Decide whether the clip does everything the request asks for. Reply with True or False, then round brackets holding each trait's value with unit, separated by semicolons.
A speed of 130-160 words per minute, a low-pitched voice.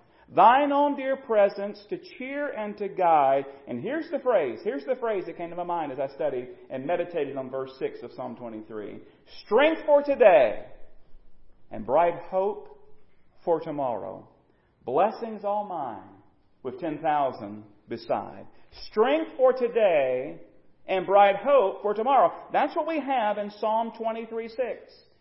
False (150 wpm; 210 Hz)